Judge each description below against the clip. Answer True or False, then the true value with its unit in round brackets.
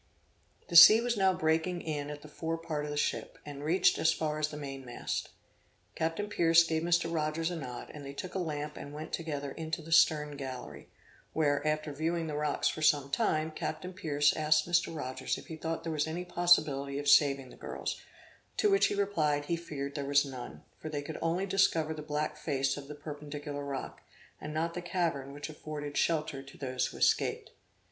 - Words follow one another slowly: False (205 wpm)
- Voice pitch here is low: False (155 Hz)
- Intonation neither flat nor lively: False (2.3 semitones)